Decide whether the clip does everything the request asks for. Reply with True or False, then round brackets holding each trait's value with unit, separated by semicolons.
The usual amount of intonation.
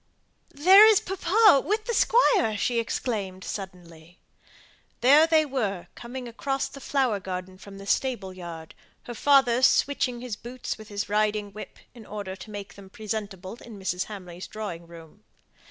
False (5.7 semitones)